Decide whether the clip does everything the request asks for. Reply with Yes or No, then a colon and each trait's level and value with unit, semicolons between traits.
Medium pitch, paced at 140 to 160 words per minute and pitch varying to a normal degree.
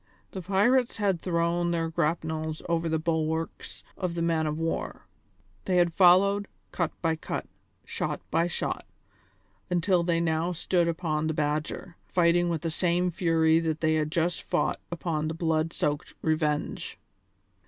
No: medium, 165 Hz; average, 155 wpm; narrow, 1.7 semitones